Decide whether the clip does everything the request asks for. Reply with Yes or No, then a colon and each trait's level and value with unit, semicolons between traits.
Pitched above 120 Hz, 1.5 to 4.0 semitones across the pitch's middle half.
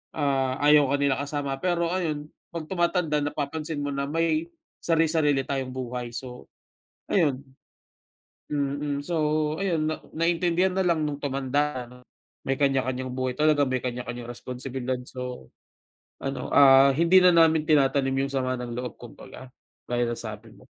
Yes: medium, 140 Hz; average, 3.4 semitones